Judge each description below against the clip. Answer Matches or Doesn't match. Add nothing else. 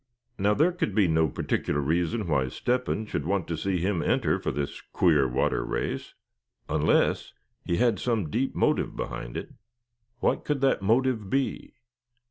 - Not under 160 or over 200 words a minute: Matches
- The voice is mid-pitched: Doesn't match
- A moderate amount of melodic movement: Doesn't match